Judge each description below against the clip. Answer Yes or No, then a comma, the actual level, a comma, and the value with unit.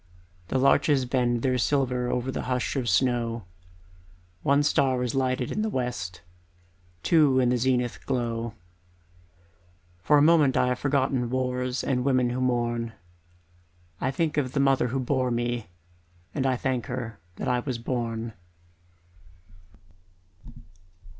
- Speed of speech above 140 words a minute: No, slow, 135 wpm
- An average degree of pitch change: No, narrow, 1.7 semitones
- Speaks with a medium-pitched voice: No, low, 125 Hz